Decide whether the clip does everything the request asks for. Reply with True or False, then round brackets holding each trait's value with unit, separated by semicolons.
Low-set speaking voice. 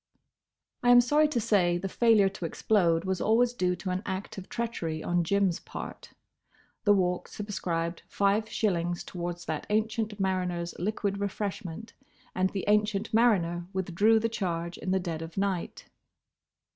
False (190 Hz)